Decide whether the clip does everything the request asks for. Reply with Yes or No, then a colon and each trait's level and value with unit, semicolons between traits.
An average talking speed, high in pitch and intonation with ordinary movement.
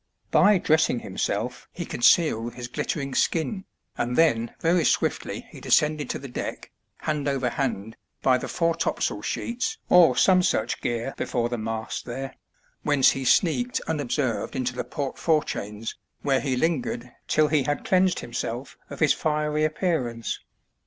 No: average, 150 wpm; medium, 140 Hz; average, 4.8 semitones